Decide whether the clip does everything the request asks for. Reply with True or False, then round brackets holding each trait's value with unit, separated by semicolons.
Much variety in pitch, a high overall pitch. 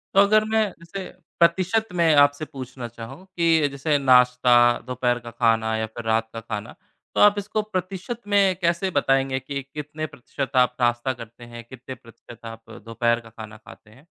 False (6.1 semitones; 130 Hz)